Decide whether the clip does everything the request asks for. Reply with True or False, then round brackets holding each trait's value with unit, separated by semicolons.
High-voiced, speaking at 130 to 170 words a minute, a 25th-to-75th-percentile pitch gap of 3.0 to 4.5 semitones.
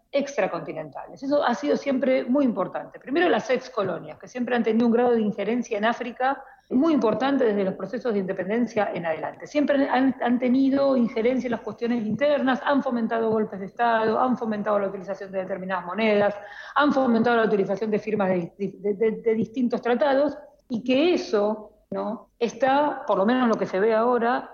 False (230 Hz; 185 wpm; 4.0 semitones)